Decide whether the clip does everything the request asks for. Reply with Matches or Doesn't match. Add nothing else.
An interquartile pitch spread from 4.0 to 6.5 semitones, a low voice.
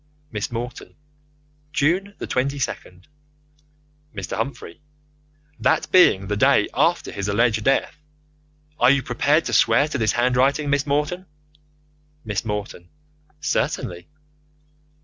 Matches